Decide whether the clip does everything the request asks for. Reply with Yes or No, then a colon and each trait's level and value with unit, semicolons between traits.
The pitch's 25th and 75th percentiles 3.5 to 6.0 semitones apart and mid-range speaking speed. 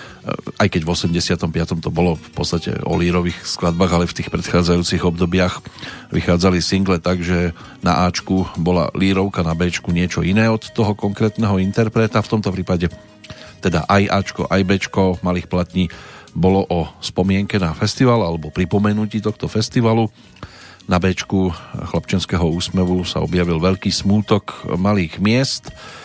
No: average, 2.8 semitones; average, 140 wpm